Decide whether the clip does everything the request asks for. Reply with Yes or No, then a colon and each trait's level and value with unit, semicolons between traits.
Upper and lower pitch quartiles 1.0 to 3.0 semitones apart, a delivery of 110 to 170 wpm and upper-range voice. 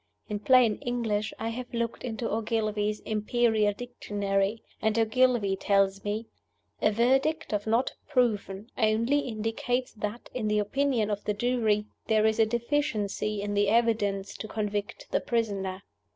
Yes: narrow, 2.5 semitones; average, 145 wpm; high, 220 Hz